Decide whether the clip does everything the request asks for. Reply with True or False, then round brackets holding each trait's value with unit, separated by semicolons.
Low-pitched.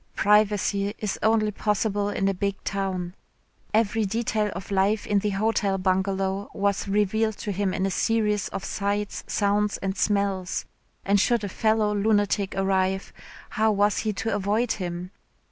False (205 Hz)